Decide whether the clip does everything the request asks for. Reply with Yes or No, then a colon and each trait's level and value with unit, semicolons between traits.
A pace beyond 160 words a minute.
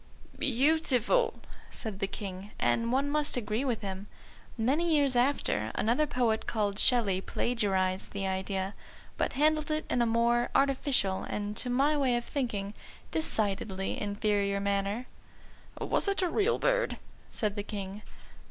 No: average, 145 wpm